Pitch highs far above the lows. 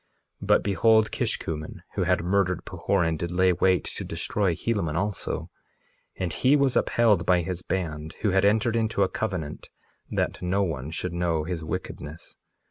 No: average, 3.5 semitones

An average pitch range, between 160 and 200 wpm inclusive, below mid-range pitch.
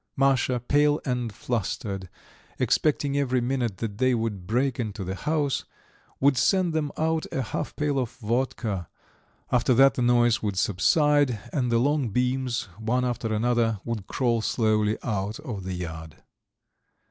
No: average, 4.0 semitones; average, 150 wpm; low, 120 Hz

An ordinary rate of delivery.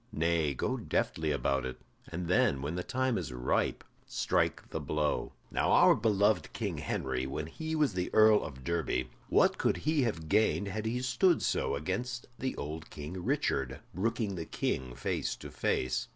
Yes: average, 175 wpm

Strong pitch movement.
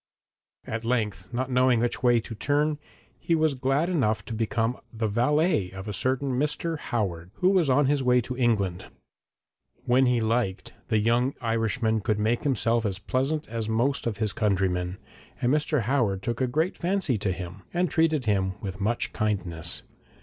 No: average, 4.4 semitones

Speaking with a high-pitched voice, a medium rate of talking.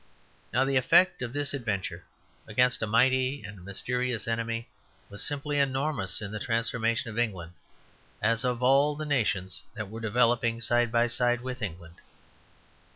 No: low, 120 Hz; average, 155 wpm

